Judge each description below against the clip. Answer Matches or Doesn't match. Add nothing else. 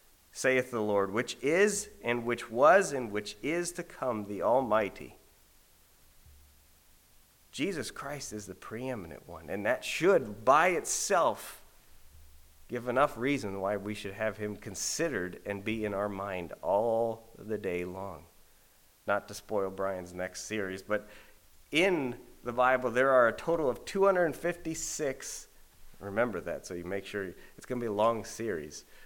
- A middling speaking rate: Matches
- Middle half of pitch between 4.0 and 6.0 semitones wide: Matches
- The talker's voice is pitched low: Matches